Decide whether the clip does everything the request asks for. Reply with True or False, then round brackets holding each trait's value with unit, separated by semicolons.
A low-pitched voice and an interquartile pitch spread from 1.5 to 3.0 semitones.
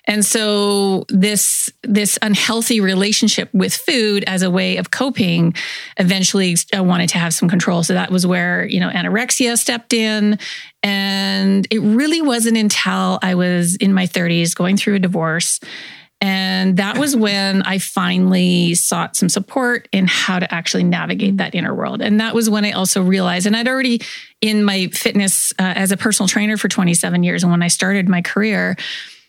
False (195 Hz; 2.7 semitones)